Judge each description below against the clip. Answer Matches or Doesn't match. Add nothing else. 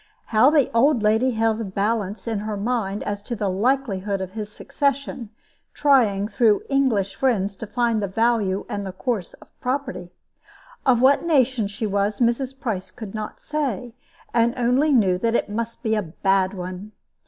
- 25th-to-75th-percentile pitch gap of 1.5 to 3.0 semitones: Doesn't match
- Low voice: Doesn't match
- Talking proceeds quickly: Doesn't match